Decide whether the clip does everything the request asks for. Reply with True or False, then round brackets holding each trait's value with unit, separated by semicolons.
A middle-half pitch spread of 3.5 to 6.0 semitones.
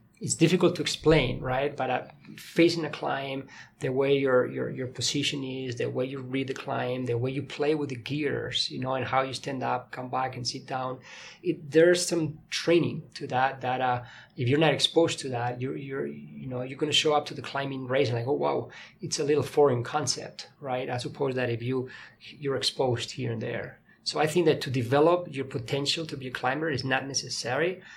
False (2.8 semitones)